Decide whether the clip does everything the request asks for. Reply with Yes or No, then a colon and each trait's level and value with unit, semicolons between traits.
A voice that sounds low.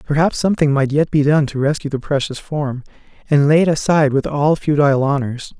No: medium, 145 Hz